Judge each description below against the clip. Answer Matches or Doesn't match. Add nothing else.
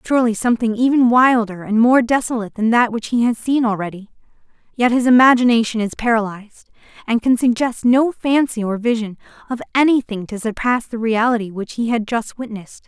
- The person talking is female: Matches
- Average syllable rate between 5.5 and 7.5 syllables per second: Matches